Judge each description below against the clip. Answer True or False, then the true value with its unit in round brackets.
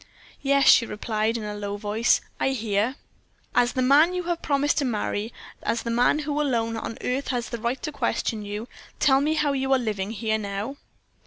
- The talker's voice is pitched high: True (240 Hz)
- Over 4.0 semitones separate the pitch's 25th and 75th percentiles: True (4.4 semitones)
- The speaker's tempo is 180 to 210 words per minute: True (200 wpm)